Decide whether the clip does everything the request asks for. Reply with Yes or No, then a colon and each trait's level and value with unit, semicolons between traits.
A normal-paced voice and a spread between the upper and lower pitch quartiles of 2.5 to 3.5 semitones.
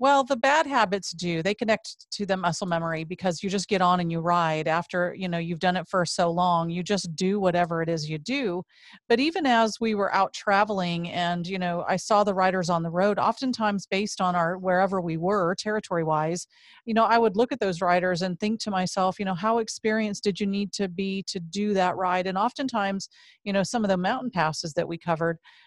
No: fast, 230 wpm; average, 3.1 semitones